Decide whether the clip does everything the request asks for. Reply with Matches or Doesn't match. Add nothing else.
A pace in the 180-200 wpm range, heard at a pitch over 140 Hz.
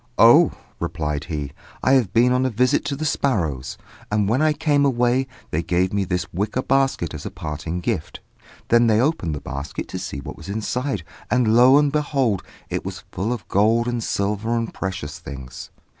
Doesn't match